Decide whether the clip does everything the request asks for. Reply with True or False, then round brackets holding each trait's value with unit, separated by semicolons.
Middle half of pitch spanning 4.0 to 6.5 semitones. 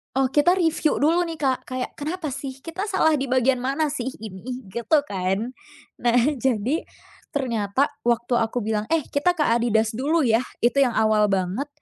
True (4.7 semitones)